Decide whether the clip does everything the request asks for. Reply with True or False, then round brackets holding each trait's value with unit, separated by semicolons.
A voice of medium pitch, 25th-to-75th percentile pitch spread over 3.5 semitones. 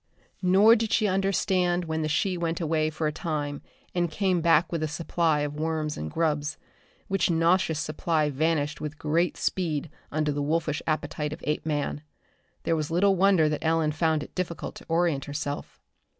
False (160 Hz; 2.5 semitones)